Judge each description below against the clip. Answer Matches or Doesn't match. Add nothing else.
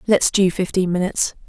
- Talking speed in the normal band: Matches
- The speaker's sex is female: Matches